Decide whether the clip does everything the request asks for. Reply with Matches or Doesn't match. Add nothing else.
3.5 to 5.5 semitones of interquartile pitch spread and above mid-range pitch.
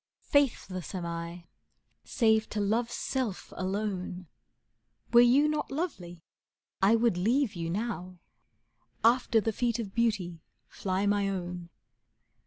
Matches